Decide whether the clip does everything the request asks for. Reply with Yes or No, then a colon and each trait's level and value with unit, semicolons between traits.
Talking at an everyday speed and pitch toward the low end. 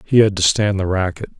No: fast, 260 wpm; very low, 95 Hz